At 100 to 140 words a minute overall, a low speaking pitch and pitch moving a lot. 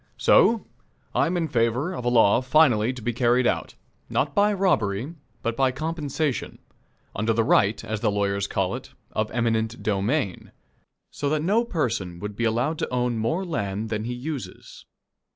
No: average, 170 wpm; low, 120 Hz; wide, 5.8 semitones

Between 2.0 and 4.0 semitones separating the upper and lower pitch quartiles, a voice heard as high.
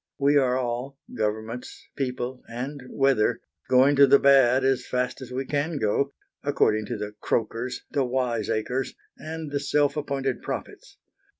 No: narrow, 2.5 semitones; low, 130 Hz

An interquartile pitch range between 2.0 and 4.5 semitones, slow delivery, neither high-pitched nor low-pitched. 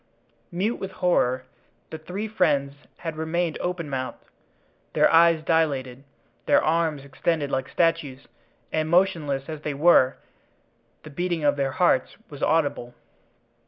Yes: average, 3.6 semitones; slow, 130 wpm; medium, 155 Hz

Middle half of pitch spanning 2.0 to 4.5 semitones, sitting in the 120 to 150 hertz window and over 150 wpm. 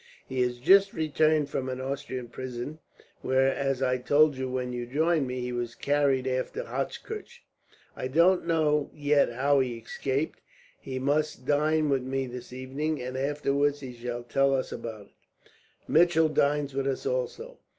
Yes: average, 2.8 semitones; low, 135 Hz; average, 165 wpm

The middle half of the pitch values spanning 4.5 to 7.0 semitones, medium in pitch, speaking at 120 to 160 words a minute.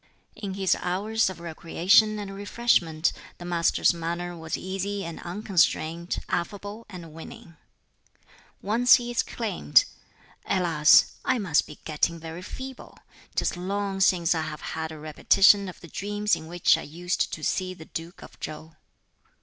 No: average, 3.7 semitones; medium, 180 Hz; average, 150 wpm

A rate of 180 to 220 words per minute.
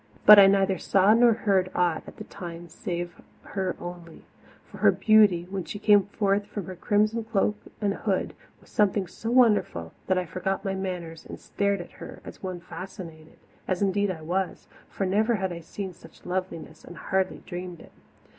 Yes: average, 185 wpm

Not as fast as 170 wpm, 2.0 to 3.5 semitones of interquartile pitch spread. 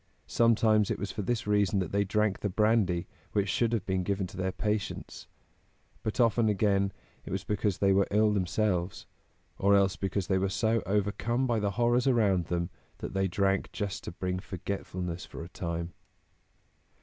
No: average, 180 wpm; narrow, 2.4 semitones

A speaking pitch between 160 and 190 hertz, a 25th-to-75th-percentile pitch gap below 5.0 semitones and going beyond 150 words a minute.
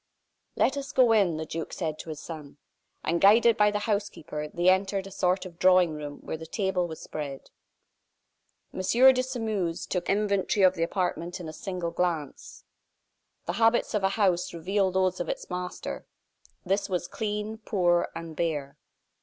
Yes: medium, 185 Hz; average, 3.5 semitones; average, 175 wpm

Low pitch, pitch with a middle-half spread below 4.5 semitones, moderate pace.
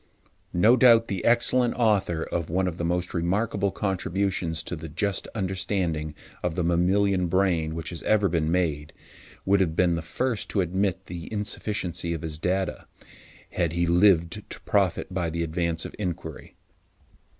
Yes: very low, 90 Hz; average, 3.0 semitones; average, 160 wpm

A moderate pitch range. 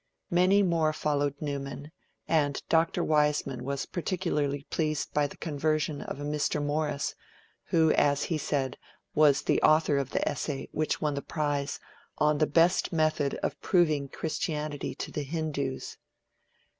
No: narrow, 1.8 semitones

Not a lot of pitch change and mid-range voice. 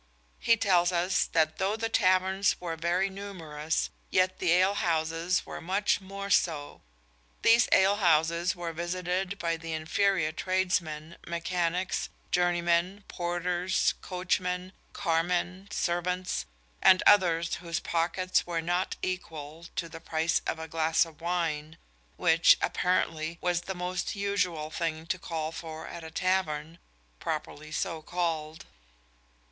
Yes: narrow, 2.2 semitones; medium, 175 Hz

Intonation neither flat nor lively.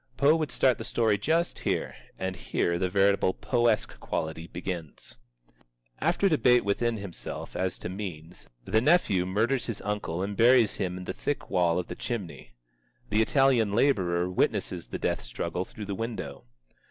Yes: average, 4.8 semitones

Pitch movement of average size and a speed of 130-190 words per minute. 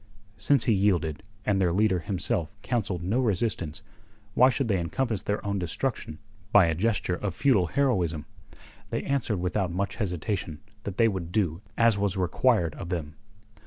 Yes: average, 4.3 semitones; average, 160 wpm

